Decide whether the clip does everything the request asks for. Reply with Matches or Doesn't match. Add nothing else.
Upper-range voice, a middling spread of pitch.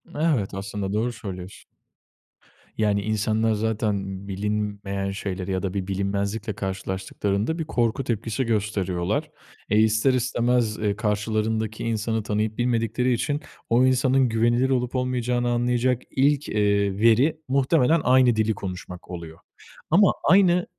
Doesn't match